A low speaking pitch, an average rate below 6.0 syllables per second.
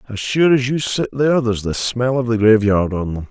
Yes: low, 120 Hz; 5.5 syllables/s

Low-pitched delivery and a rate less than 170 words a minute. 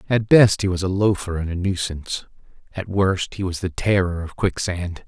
No: very low, 95 Hz; average, 200 wpm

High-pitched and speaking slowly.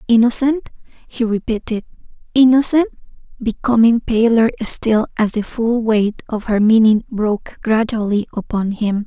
Yes: high, 225 Hz; slow, 120 wpm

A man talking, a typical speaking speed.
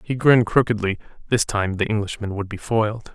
Yes: male; average, 190 wpm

